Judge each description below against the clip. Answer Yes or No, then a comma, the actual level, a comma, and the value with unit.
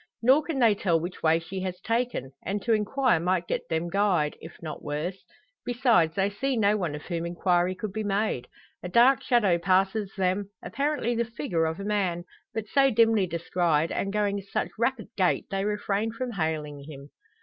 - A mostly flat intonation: No, average, 4.6 semitones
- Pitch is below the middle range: No, high, 195 Hz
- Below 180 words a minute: No, average, 195 wpm